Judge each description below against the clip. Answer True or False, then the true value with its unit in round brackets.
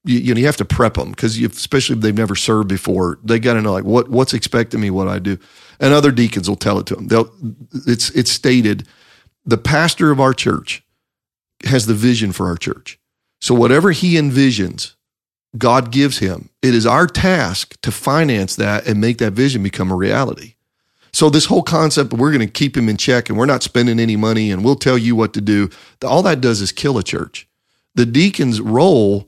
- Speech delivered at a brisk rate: True (215 wpm)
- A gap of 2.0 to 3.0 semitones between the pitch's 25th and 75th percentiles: False (4.2 semitones)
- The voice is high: False (120 Hz)